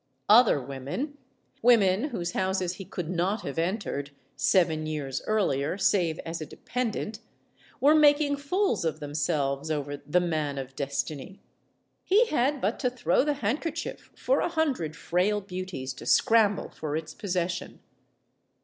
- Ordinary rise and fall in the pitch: No, wide, 7.7 semitones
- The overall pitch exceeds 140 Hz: Yes, medium, 185 Hz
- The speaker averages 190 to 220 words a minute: No, average, 140 wpm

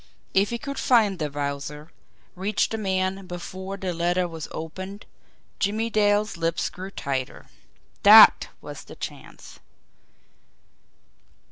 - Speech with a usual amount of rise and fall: Yes, average, 3.8 semitones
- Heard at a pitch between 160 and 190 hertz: Yes, medium, 185 Hz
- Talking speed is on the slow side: Yes, slow, 120 wpm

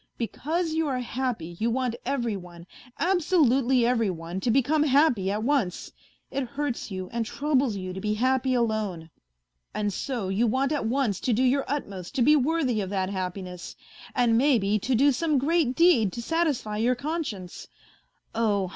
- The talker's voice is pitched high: Yes, high, 240 Hz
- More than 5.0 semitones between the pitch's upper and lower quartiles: Yes, wide, 5.5 semitones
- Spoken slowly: No, average, 175 wpm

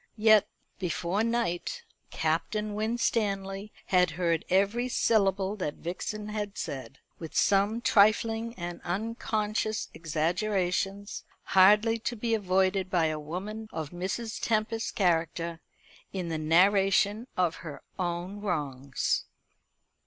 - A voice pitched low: No, high, 195 Hz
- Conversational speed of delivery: No, slow, 110 wpm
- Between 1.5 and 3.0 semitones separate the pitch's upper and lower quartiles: No, average, 3.8 semitones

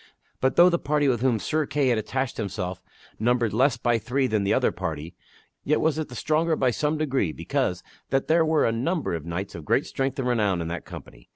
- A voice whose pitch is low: Yes, low, 125 Hz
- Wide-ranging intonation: Yes, wide, 6.3 semitones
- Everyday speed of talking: No, fast, 225 wpm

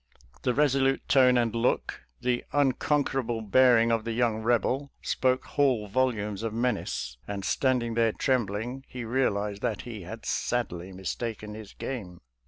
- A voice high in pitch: No, low, 120 Hz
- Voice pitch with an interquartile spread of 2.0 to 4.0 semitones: Yes, average, 3.4 semitones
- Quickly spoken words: No, average, 155 wpm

